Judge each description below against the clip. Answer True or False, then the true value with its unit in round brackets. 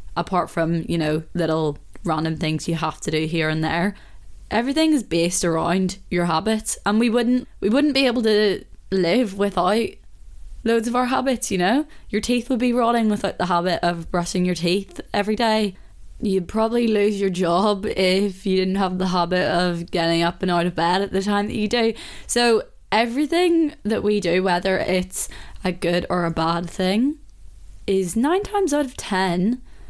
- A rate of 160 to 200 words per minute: True (185 wpm)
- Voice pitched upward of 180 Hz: True (190 Hz)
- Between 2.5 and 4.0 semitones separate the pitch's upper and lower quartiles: False (4.7 semitones)